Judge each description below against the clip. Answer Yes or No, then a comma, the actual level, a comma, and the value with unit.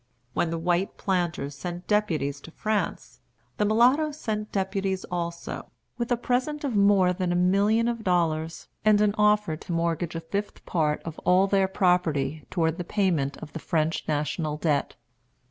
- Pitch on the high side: No, medium, 180 Hz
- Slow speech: No, average, 165 wpm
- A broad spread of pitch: No, average, 4.3 semitones